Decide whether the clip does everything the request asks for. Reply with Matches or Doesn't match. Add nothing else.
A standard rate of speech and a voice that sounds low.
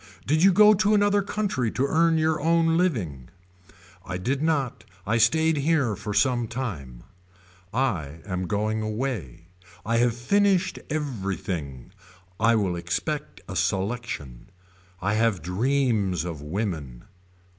Doesn't match